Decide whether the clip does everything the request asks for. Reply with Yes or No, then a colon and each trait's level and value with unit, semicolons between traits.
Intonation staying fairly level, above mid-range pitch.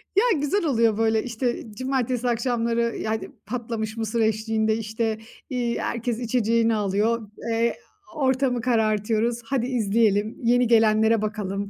Yes: narrow, 1.9 semitones; high, 230 Hz